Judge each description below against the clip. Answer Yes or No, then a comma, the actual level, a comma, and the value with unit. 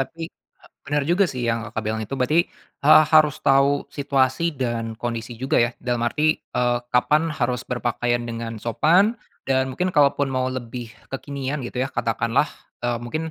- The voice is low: Yes, low, 130 Hz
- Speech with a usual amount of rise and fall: Yes, average, 3.3 semitones